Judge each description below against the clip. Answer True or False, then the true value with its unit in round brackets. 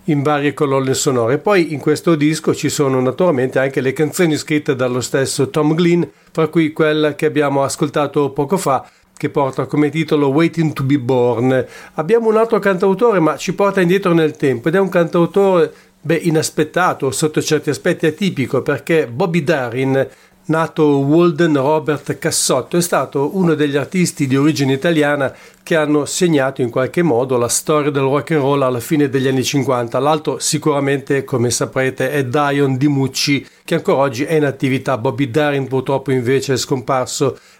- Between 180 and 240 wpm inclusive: False (170 wpm)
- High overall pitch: False (150 Hz)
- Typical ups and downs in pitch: True (3.1 semitones)